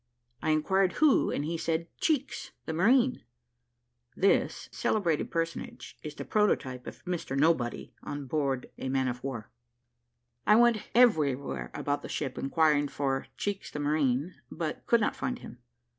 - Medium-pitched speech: Yes, medium, 155 Hz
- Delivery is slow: No, average, 155 wpm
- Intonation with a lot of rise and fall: Yes, wide, 6.2 semitones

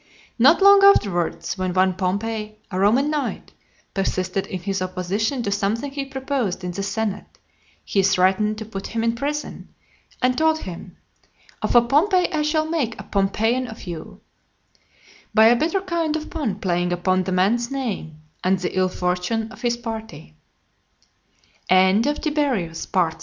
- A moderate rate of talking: Yes, average, 150 wpm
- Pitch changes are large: Yes, wide, 6.5 semitones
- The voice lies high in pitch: Yes, high, 220 Hz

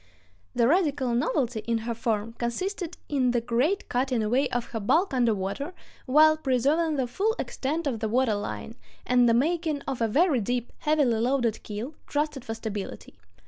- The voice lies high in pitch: Yes, very high, 250 Hz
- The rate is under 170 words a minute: No, average, 175 wpm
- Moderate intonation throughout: Yes, average, 4.5 semitones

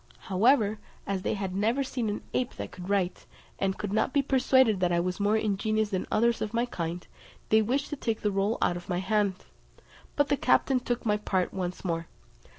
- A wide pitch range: No, average, 3.9 semitones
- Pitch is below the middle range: No, high, 210 Hz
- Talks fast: Yes, fast, 210 wpm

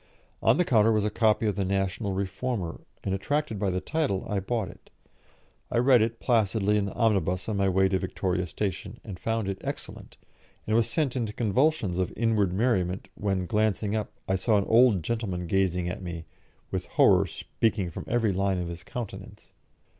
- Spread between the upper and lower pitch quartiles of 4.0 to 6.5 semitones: No, average, 3.2 semitones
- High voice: No, low, 100 Hz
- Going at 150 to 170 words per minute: No, average, 190 wpm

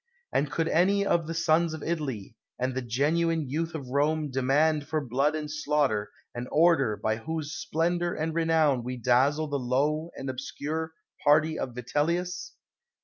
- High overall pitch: No, medium, 150 Hz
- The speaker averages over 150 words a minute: Yes, average, 160 wpm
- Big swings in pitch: No, average, 3.7 semitones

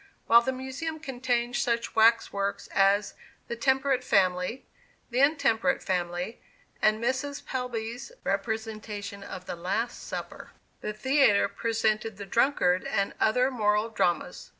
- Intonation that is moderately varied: Yes, average, 4.1 semitones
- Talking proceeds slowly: Yes, slow, 125 wpm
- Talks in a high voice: Yes, high, 225 Hz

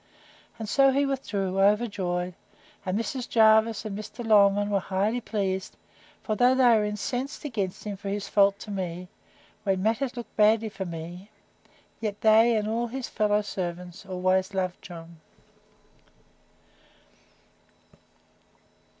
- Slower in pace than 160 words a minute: Yes, slow, 135 wpm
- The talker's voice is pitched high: Yes, high, 205 Hz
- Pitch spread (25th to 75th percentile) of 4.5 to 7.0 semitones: No, average, 3.1 semitones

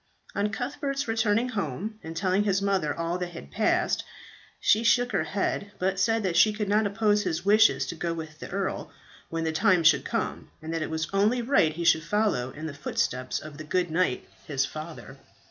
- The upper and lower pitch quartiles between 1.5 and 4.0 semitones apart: No, average, 4.8 semitones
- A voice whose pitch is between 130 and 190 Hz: Yes, medium, 185 Hz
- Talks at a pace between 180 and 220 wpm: Yes, fast, 205 wpm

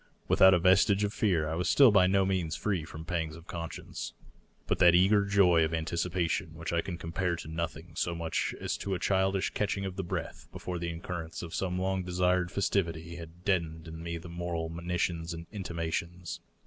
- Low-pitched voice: Yes, very low, 85 Hz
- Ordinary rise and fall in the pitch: No, narrow, 2.3 semitones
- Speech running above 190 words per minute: Yes, average, 200 wpm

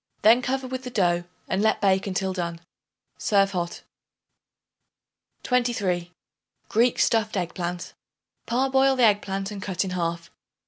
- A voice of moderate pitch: No, high, 195 Hz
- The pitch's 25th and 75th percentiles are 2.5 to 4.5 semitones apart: No, average, 5.0 semitones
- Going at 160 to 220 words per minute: No, average, 140 wpm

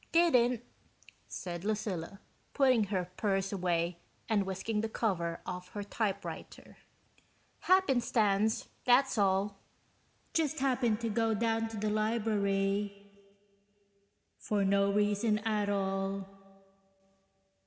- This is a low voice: No, high, 205 Hz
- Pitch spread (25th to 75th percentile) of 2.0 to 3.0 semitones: Yes, narrow, 2.5 semitones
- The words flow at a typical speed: No, slow, 100 wpm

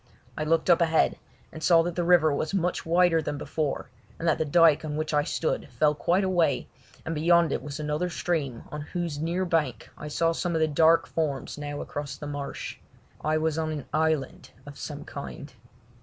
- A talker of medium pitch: Yes, medium, 160 Hz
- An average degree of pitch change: No, narrow, 2.2 semitones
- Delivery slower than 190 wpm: No, average, 200 wpm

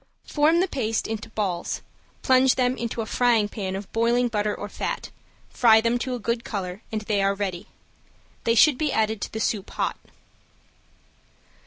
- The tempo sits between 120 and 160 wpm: No, average, 175 wpm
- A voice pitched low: No, high, 220 Hz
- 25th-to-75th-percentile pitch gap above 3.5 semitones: No, average, 2.9 semitones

